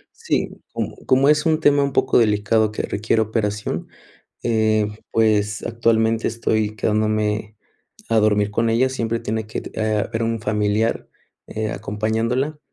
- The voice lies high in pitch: No, low, 110 Hz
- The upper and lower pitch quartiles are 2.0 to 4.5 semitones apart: No, narrow, 1.4 semitones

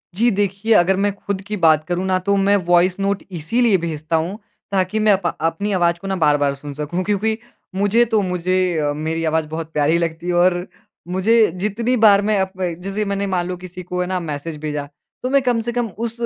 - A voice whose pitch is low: No, medium, 185 Hz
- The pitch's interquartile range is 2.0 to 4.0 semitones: Yes, average, 3.6 semitones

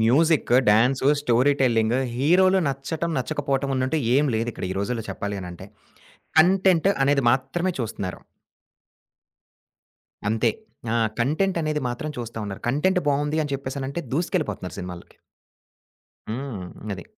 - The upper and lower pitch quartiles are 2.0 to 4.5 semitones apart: No, average, 5.0 semitones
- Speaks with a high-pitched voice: No, low, 135 Hz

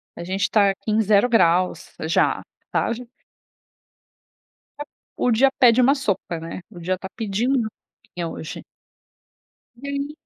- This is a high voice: Yes, high, 210 Hz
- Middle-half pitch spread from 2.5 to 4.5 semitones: No, average, 5.3 semitones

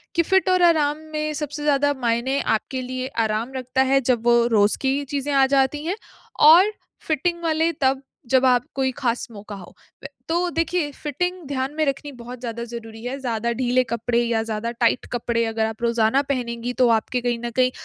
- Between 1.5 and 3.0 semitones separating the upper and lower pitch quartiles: No, average, 3.7 semitones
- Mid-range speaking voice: No, very high, 255 Hz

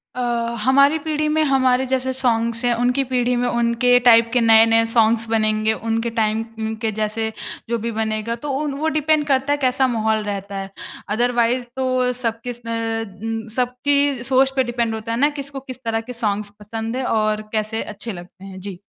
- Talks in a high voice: Yes, high, 235 Hz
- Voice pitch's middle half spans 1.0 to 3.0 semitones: Yes, average, 2.7 semitones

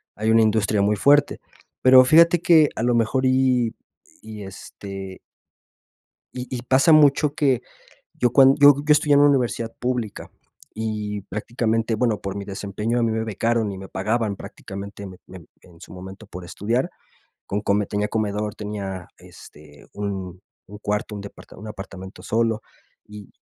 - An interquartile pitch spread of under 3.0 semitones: No, average, 3.7 semitones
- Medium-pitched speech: No, low, 110 Hz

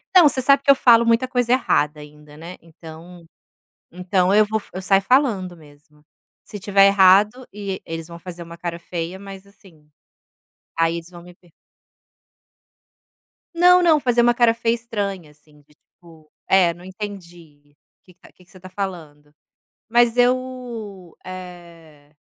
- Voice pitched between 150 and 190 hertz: Yes, medium, 185 Hz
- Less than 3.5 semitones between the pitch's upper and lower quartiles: No, wide, 5.4 semitones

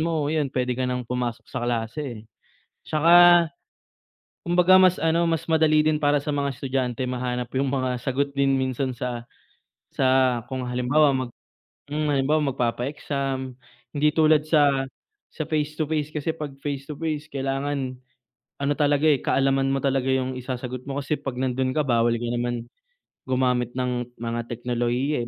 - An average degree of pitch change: Yes, average, 3.0 semitones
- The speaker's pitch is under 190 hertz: Yes, low, 135 Hz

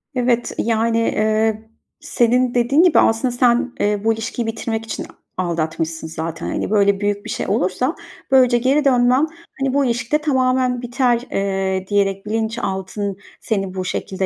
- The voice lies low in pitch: No, high, 225 Hz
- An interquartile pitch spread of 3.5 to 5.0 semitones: Yes, average, 4.0 semitones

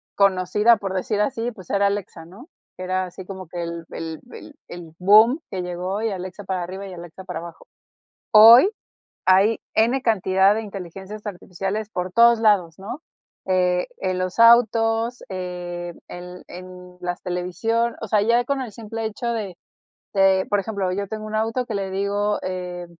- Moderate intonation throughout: Yes, average, 3.4 semitones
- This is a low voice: No, high, 195 Hz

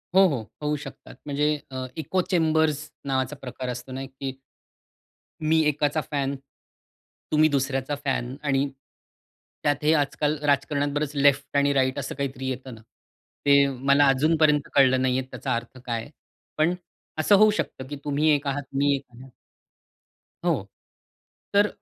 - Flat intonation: Yes, narrow, 2.1 semitones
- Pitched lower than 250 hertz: Yes, medium, 140 Hz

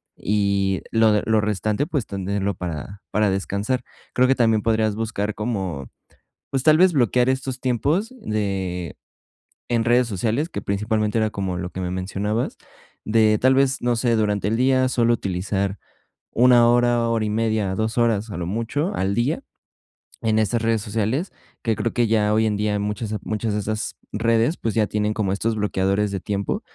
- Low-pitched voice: Yes, low, 110 Hz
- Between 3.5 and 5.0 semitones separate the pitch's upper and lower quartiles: No, average, 2.8 semitones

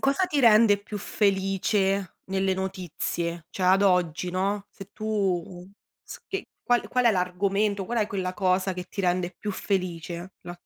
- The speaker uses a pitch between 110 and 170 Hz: No, high, 190 Hz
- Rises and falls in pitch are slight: Yes, narrow, 2.3 semitones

